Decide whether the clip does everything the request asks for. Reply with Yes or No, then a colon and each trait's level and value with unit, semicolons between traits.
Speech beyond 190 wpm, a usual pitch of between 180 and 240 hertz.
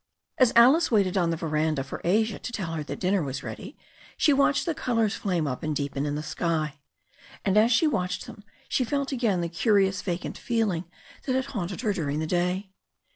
Yes: fast, 205 wpm; high, 190 Hz